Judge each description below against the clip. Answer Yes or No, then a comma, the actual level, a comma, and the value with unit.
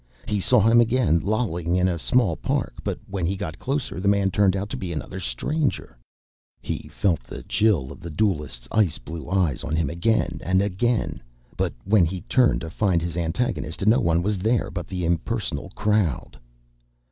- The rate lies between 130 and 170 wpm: No, average, 185 wpm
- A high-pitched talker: No, very low, 95 Hz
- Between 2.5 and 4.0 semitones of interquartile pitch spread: No, average, 4.4 semitones